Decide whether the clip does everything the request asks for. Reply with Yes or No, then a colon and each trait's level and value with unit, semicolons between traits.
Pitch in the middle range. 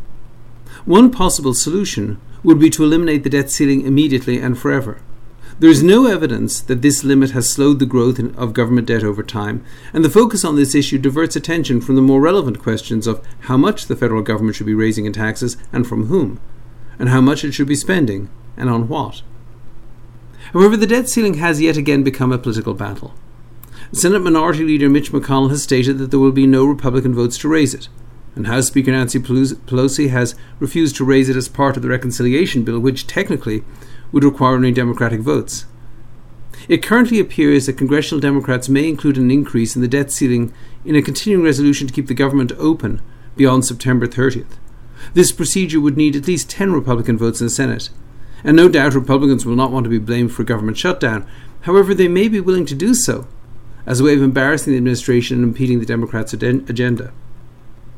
No: low, 130 Hz